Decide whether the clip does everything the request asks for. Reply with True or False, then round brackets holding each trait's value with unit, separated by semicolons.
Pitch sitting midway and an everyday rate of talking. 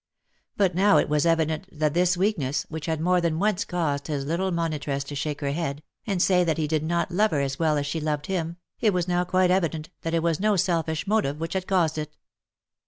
False (165 Hz; 235 wpm)